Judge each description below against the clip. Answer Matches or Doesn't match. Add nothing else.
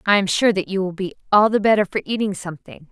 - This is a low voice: Doesn't match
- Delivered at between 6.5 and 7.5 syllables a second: Matches